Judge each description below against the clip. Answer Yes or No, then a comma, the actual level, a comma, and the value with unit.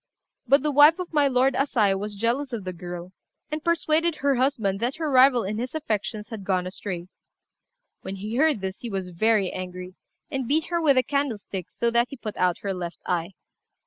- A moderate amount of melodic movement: No, wide, 6.5 semitones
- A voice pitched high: Yes, high, 230 Hz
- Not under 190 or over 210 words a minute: Yes, fast, 205 wpm